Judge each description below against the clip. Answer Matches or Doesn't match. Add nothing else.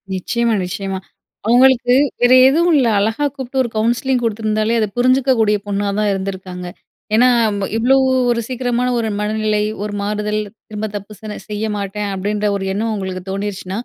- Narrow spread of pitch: Doesn't match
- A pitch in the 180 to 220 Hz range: Matches